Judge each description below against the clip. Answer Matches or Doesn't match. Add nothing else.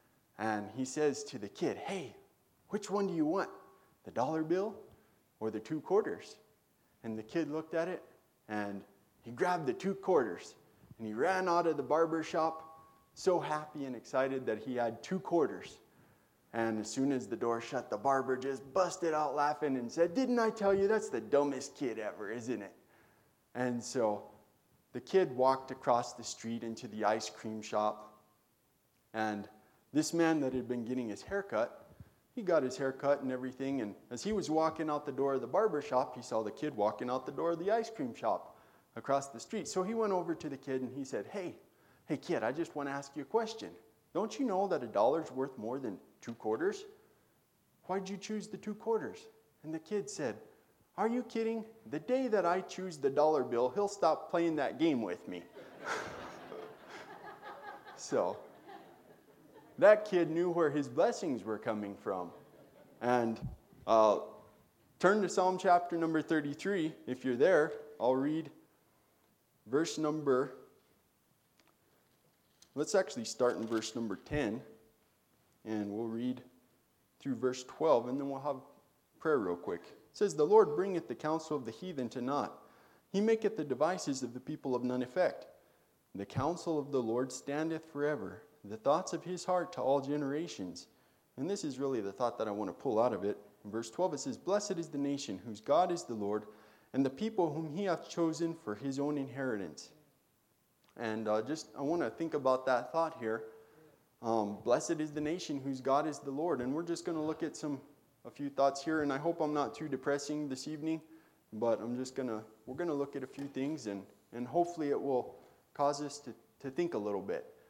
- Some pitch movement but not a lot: Doesn't match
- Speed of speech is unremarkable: Matches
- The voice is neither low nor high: Matches